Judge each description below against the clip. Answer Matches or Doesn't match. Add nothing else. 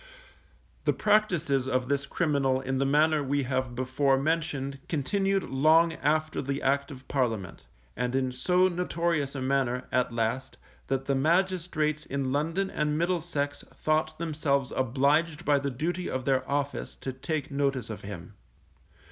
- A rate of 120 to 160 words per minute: Matches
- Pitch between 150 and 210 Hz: Doesn't match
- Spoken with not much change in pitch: Doesn't match